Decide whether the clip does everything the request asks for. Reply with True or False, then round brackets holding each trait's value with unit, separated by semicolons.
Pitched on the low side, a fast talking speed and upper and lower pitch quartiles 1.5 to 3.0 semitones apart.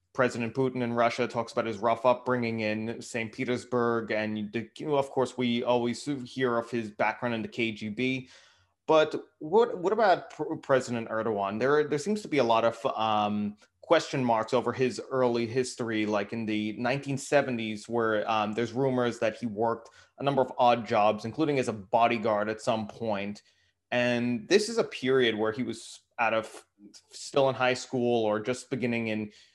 True (120 Hz; 175 wpm; 2.5 semitones)